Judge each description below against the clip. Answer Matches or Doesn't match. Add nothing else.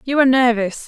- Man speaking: Doesn't match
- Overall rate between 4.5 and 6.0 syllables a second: Doesn't match